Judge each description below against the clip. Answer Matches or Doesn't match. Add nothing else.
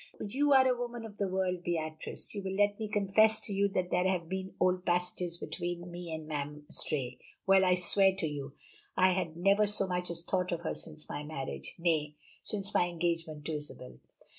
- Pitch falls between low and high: Matches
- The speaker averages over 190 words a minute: Matches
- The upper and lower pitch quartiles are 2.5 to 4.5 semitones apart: Matches